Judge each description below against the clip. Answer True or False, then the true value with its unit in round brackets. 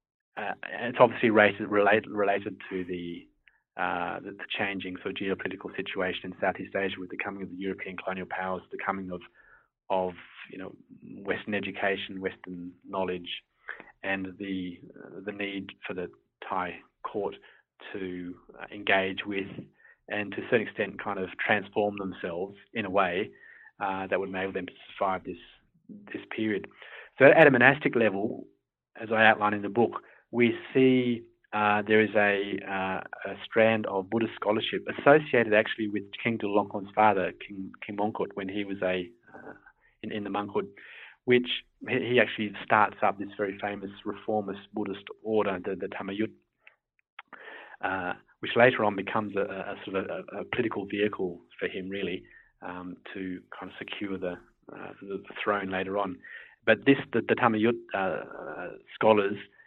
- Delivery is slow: False (165 wpm)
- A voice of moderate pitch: False (100 Hz)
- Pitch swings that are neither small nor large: False (2.1 semitones)